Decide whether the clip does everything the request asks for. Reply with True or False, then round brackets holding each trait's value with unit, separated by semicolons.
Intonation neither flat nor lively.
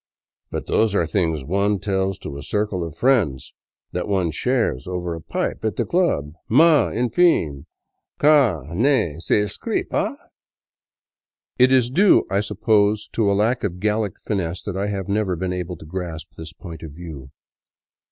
True (4.7 semitones)